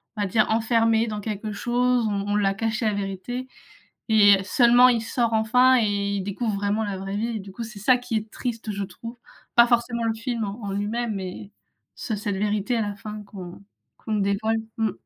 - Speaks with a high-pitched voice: Yes, high, 215 Hz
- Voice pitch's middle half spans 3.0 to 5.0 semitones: No, narrow, 2.5 semitones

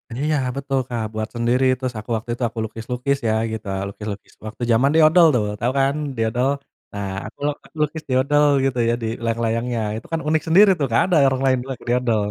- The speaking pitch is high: No, low, 125 Hz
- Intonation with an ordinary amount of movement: Yes, average, 3.5 semitones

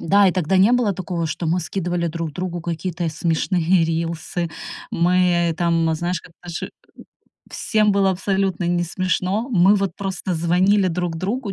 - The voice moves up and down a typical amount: No, narrow, 2.2 semitones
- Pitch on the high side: No, medium, 180 Hz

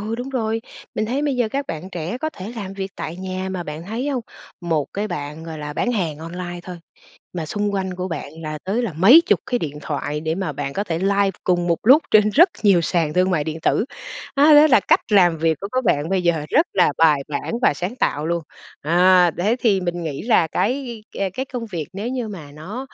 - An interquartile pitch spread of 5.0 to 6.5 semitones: Yes, wide, 5.6 semitones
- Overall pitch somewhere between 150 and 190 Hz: Yes, medium, 185 Hz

